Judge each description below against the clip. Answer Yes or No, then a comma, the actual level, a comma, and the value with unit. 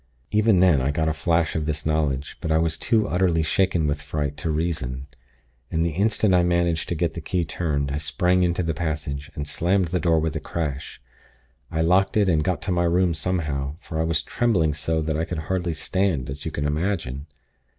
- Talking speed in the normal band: No, fast, 215 wpm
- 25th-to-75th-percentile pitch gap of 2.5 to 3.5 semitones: Yes, average, 3.0 semitones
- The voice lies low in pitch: Yes, very low, 80 Hz